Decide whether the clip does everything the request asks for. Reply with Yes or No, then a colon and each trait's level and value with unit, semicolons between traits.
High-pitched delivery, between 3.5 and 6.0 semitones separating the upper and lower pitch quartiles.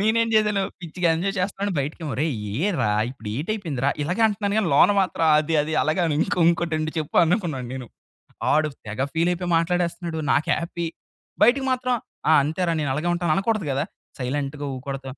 No: medium, 165 Hz; average, 4.6 semitones